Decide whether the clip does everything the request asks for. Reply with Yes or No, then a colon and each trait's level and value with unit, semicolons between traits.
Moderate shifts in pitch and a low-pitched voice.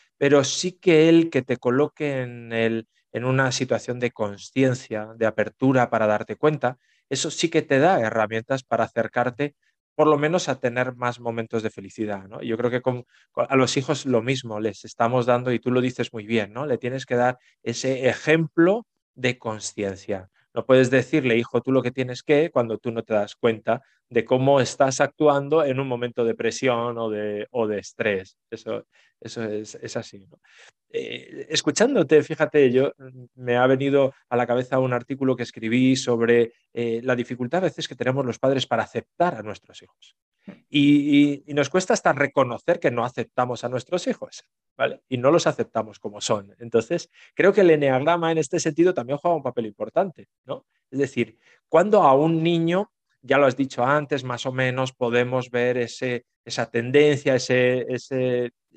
Yes: average, 3.6 semitones; low, 125 Hz